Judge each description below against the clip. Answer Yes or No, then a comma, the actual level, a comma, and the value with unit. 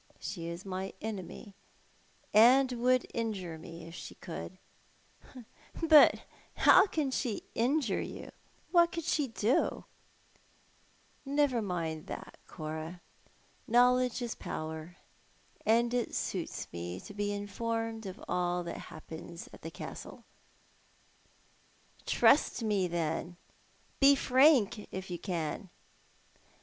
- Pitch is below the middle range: No, high, 205 Hz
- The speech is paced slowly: Yes, slow, 120 wpm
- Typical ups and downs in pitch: No, wide, 6.4 semitones